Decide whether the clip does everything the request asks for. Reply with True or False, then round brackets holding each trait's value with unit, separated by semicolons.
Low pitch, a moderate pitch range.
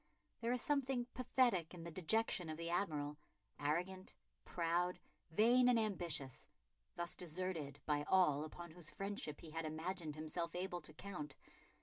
False (175 Hz; 3.9 semitones)